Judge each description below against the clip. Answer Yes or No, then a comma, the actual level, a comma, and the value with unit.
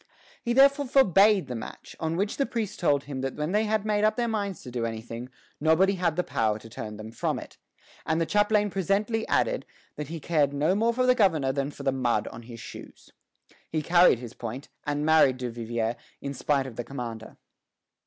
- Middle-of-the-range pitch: Yes, medium, 155 Hz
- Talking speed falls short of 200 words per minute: No, fast, 205 wpm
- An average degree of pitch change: No, wide, 8.7 semitones